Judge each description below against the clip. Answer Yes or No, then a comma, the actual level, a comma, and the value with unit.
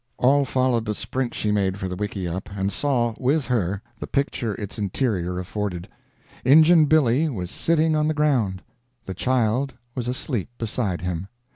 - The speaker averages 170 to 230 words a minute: No, average, 160 wpm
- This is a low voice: Yes, low, 115 Hz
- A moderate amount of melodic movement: No, wide, 6.0 semitones